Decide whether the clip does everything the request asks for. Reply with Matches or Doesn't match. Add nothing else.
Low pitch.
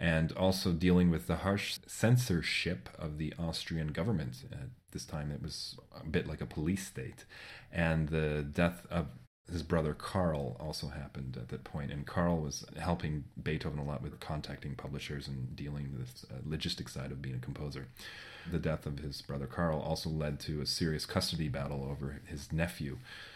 Matches